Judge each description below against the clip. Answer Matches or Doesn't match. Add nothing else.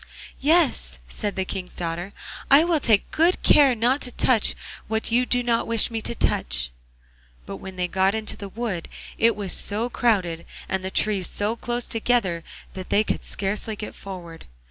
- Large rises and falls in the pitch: Doesn't match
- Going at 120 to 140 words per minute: Doesn't match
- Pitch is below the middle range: Doesn't match